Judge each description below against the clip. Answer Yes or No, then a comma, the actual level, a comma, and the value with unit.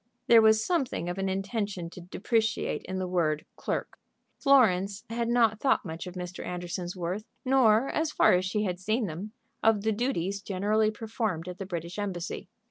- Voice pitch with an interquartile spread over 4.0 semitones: No, average, 3.6 semitones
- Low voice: No, high, 200 Hz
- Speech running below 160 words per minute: No, average, 180 wpm